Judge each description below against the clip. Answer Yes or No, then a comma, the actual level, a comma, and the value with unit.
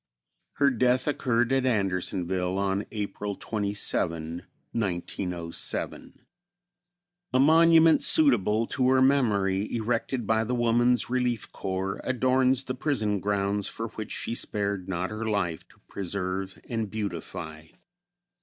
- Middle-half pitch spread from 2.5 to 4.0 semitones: No, average, 4.5 semitones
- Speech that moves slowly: Yes, slow, 115 wpm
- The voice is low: Yes, low, 105 Hz